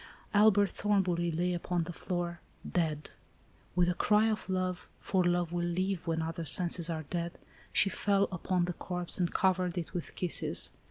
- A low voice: No, medium, 175 Hz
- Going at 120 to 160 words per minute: No, average, 170 wpm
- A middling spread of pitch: No, narrow, 1.6 semitones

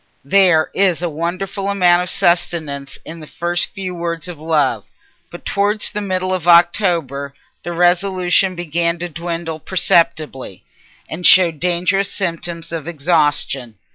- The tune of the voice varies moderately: No, narrow, 2.3 semitones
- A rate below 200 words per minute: Yes, average, 140 wpm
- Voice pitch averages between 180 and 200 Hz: No, medium, 170 Hz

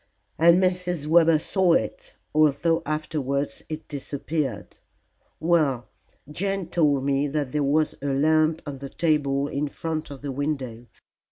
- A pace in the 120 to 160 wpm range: Yes, average, 140 wpm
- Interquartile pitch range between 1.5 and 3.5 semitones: Yes, average, 2.7 semitones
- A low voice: No, medium, 150 Hz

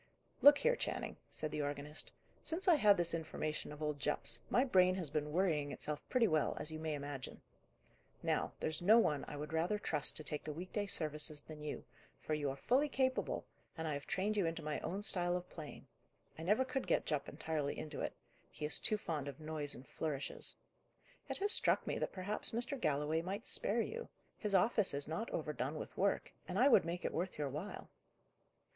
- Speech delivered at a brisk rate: Yes, fast, 210 wpm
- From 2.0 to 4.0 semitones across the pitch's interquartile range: No, average, 5.3 semitones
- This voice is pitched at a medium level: Yes, medium, 160 Hz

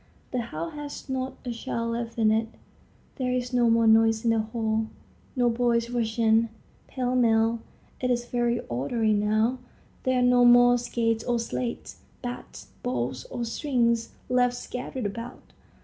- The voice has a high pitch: Yes, high, 235 Hz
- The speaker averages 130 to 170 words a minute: Yes, average, 160 wpm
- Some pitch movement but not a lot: No, narrow, 1.7 semitones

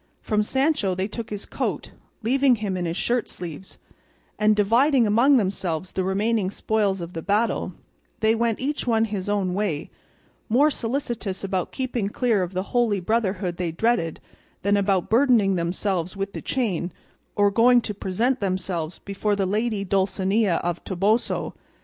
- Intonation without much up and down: No, average, 3.7 semitones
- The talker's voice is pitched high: Yes, high, 205 Hz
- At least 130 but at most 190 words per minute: Yes, average, 160 wpm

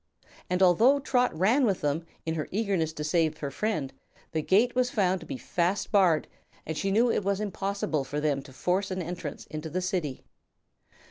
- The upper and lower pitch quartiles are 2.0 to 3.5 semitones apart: No, average, 4.5 semitones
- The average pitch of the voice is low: No, medium, 180 Hz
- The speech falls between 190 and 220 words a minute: Yes, average, 195 wpm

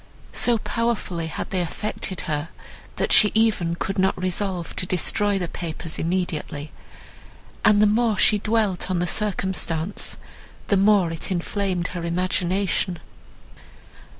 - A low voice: No, medium, 185 Hz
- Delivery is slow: Yes, slow, 130 wpm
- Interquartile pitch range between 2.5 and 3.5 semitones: Yes, average, 3.2 semitones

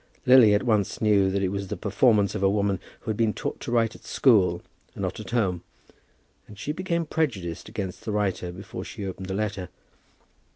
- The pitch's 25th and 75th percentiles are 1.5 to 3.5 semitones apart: Yes, average, 2.9 semitones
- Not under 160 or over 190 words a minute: No, fast, 205 wpm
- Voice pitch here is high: No, low, 105 Hz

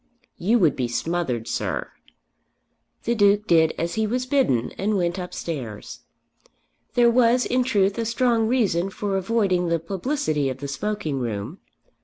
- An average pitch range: No, wide, 6.4 semitones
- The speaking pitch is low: No, high, 195 Hz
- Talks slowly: No, average, 150 wpm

